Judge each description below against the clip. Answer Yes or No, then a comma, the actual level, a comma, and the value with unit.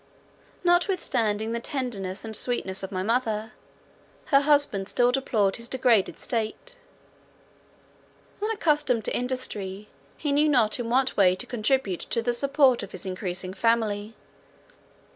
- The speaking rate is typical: No, slow, 130 wpm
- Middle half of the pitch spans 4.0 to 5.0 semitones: Yes, average, 4.5 semitones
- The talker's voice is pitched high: Yes, high, 230 Hz